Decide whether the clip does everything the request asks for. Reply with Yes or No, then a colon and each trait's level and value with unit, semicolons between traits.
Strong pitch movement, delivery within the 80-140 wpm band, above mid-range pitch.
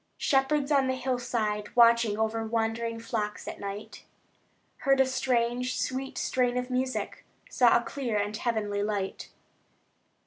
No: average, 3.0 semitones; slow, 135 wpm; high, 235 Hz